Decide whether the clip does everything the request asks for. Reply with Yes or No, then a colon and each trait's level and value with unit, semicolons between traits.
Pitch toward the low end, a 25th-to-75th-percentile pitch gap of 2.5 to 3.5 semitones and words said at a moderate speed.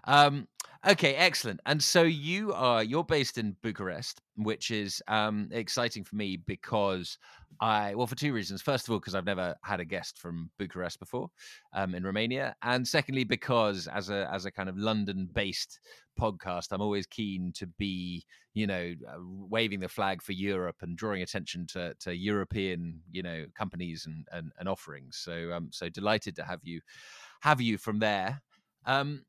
No: low, 100 Hz; average, 4.2 semitones; average, 180 wpm